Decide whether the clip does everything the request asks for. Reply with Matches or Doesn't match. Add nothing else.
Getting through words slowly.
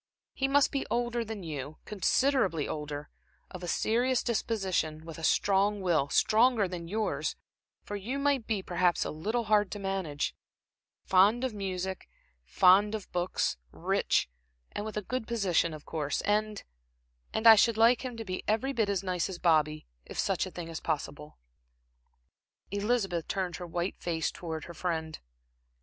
Doesn't match